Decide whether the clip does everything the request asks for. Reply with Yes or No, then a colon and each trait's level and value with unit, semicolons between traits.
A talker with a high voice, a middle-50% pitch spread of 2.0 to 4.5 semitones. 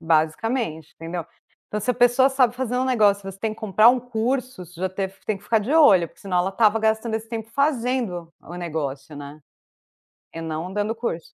No: high, 210 Hz; wide, 5.6 semitones